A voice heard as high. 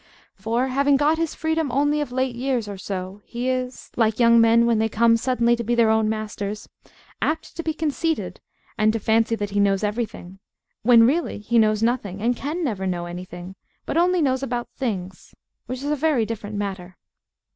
Yes: high, 235 Hz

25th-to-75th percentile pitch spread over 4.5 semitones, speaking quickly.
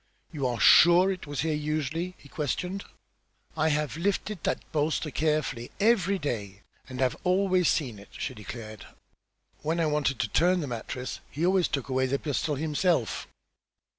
No: average, 5.1 semitones; average, 165 wpm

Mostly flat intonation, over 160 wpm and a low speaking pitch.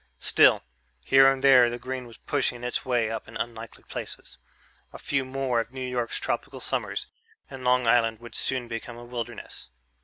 Yes: narrow, 1.8 semitones; average, 180 wpm; low, 125 Hz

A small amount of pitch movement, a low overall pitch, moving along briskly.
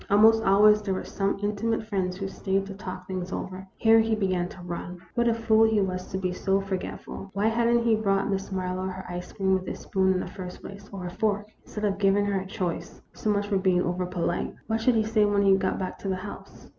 No: narrow, 2.2 semitones; high, 195 Hz; fast, 255 wpm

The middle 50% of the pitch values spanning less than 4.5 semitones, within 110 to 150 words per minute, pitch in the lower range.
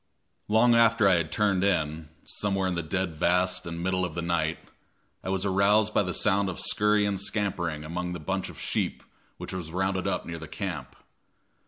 No: average, 2.9 semitones; average, 195 wpm; very low, 95 Hz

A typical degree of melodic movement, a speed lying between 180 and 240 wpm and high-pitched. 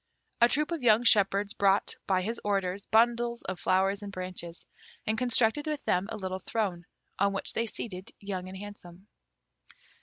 No: average, 3.5 semitones; average, 170 wpm; high, 200 Hz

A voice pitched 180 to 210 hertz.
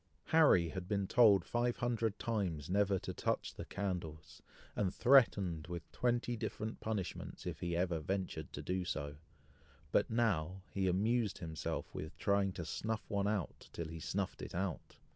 No: very low, 95 Hz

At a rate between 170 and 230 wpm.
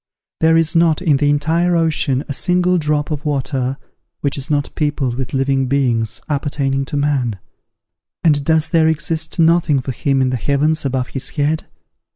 Yes: average, 175 wpm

